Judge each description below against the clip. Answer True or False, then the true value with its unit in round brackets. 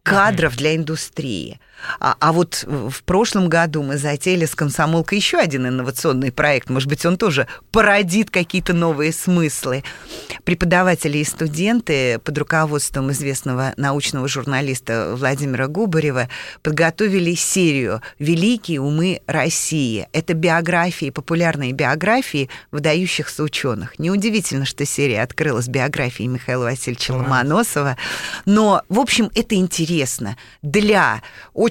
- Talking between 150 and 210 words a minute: False (115 wpm)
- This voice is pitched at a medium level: True (155 Hz)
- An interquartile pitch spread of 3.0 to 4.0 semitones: False (4.8 semitones)